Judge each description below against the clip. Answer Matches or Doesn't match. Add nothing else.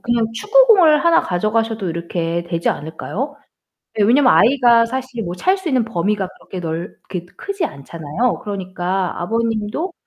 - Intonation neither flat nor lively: Doesn't match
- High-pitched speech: Matches